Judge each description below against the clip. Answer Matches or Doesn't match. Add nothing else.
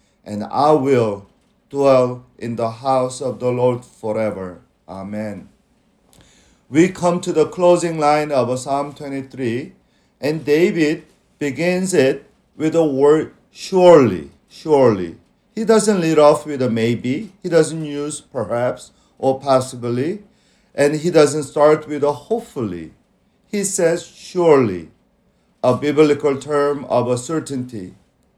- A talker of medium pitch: Matches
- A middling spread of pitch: Matches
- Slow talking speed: Matches